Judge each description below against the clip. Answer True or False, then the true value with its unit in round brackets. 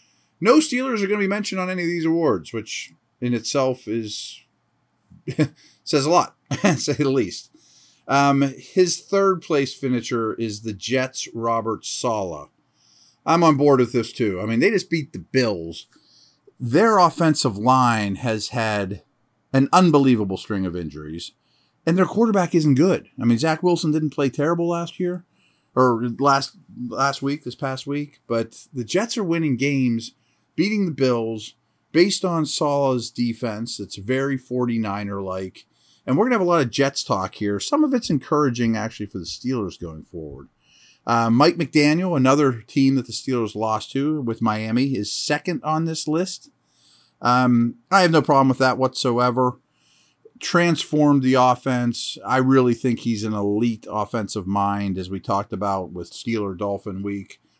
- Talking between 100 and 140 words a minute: False (165 wpm)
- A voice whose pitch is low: True (130 Hz)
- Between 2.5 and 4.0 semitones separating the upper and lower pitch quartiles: False (5.4 semitones)